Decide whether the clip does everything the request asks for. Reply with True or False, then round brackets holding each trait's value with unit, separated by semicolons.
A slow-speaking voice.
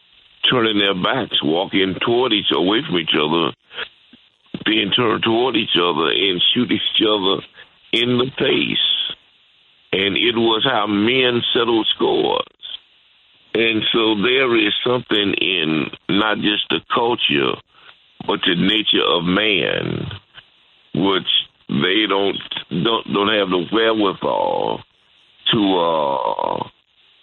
True (120 wpm)